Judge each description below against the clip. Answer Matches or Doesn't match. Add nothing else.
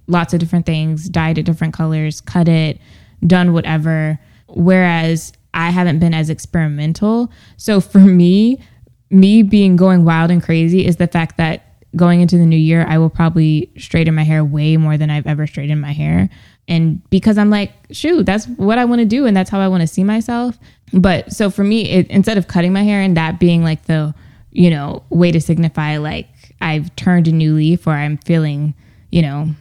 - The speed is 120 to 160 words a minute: Doesn't match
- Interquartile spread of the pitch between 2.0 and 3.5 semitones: Matches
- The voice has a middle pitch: Matches